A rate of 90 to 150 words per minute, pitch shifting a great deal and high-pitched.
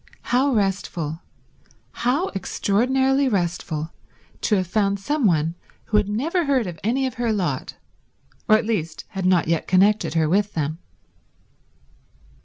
Yes: average, 140 wpm; wide, 5.9 semitones; high, 205 Hz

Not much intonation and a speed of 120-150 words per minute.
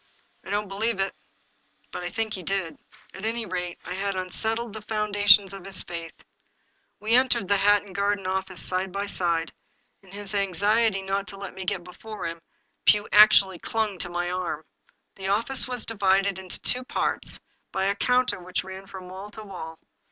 No: narrow, 2.1 semitones; average, 185 wpm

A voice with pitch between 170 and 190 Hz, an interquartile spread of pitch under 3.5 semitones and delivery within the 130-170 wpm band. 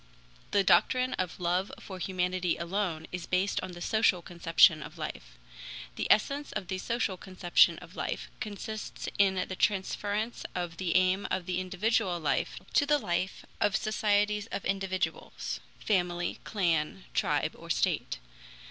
Yes: medium, 185 Hz; average, 2.7 semitones; average, 150 wpm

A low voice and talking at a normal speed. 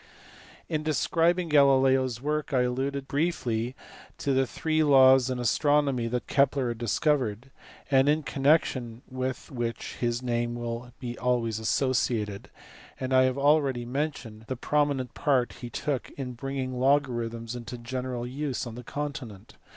Yes: low, 130 Hz; average, 150 wpm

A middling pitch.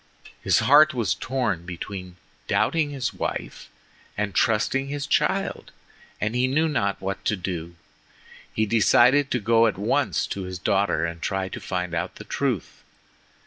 No: low, 105 Hz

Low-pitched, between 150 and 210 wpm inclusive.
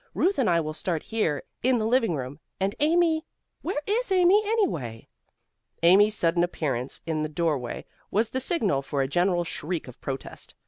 No: medium, 175 Hz; average, 175 wpm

